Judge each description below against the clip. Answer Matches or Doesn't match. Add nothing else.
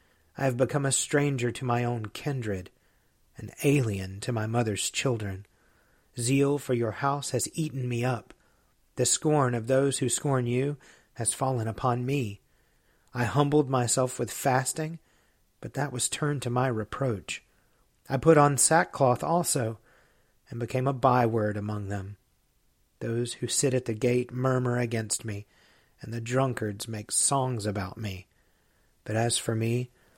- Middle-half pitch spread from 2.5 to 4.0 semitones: Matches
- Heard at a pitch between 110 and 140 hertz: Matches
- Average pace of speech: Matches